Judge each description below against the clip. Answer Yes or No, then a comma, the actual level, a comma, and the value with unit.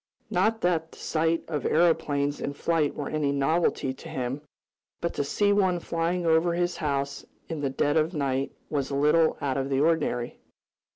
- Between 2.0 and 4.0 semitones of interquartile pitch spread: Yes, average, 3.1 semitones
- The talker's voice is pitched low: No, medium, 155 Hz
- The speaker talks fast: No, average, 180 wpm